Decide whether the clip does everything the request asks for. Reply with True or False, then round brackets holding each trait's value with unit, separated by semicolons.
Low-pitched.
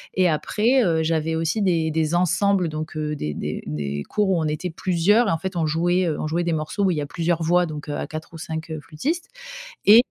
False (165 Hz)